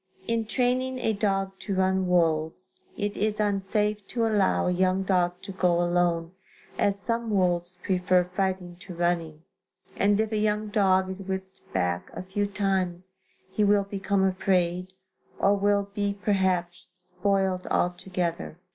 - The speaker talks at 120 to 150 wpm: Yes, average, 145 wpm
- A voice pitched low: No, high, 190 Hz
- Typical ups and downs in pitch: No, narrow, 2.3 semitones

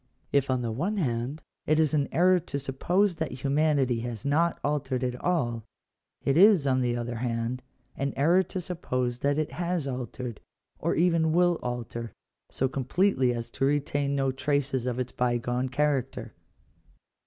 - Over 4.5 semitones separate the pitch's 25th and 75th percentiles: No, average, 4.1 semitones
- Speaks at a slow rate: No, average, 165 wpm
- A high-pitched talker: No, low, 135 Hz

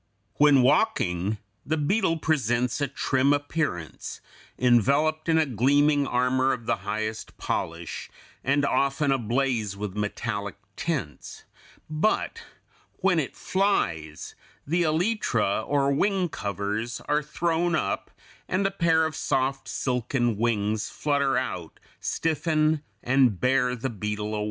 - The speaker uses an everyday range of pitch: No, wide, 5.9 semitones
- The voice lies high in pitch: No, low, 135 Hz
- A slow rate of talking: Yes, slow, 120 wpm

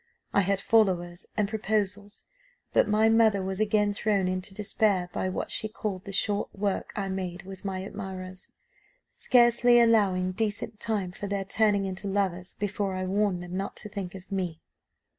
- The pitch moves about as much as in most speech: No, narrow, 2.2 semitones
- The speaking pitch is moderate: No, high, 200 Hz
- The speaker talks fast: No, average, 170 wpm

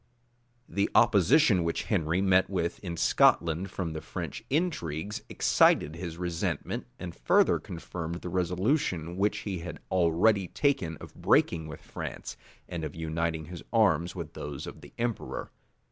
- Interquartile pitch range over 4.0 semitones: No, average, 3.2 semitones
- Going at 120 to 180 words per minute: Yes, average, 150 wpm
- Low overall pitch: Yes, very low, 85 Hz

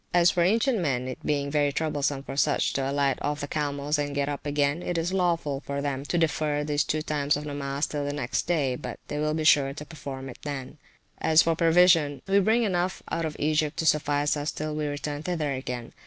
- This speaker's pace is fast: Yes, fast, 230 wpm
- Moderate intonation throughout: No, narrow, 2.2 semitones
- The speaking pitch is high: No, medium, 150 Hz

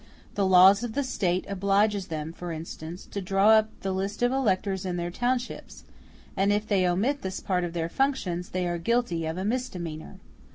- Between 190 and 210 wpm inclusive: Yes, average, 195 wpm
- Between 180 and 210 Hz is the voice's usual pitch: Yes, high, 190 Hz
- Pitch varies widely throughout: No, average, 3.6 semitones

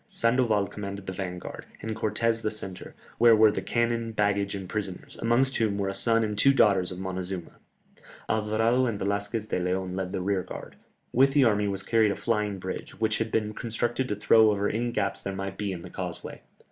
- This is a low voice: Yes, low, 105 Hz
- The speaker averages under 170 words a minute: No, average, 200 wpm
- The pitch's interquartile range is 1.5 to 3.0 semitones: Yes, average, 2.7 semitones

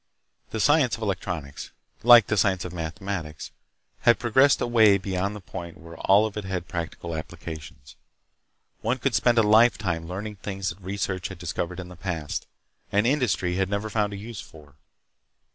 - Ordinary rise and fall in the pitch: Yes, average, 3.9 semitones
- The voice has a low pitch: Yes, very low, 95 Hz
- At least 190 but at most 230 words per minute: No, average, 170 wpm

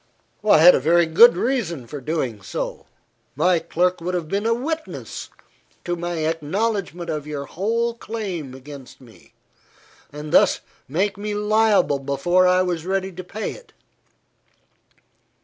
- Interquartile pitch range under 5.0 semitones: No, average, 5.3 semitones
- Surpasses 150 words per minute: No, average, 145 wpm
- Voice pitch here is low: No, medium, 175 Hz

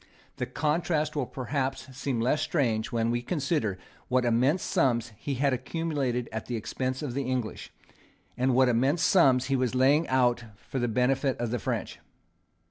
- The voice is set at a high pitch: No, low, 130 Hz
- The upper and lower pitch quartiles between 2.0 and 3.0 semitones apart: Yes, average, 2.7 semitones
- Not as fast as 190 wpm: Yes, average, 170 wpm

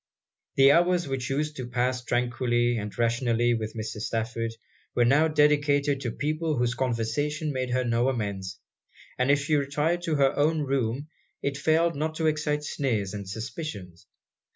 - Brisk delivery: No, average, 160 wpm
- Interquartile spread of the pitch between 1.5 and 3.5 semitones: No, average, 4.1 semitones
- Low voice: Yes, low, 130 Hz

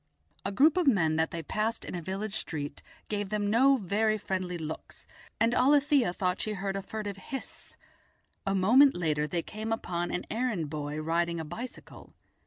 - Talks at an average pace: Yes, average, 180 wpm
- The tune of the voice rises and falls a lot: No, average, 4.7 semitones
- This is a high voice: Yes, high, 195 Hz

